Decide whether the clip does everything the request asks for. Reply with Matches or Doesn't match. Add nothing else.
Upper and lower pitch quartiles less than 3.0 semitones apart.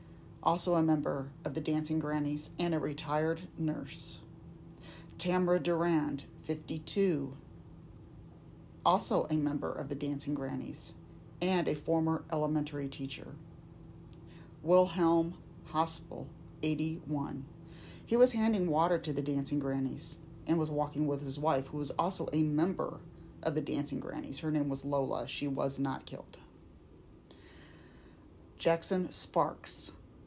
Matches